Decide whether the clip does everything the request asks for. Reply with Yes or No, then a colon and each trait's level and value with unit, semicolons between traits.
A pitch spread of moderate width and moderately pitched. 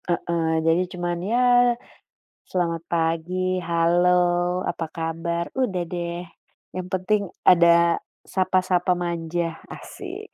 No: narrow, 1.5 semitones; medium, 175 Hz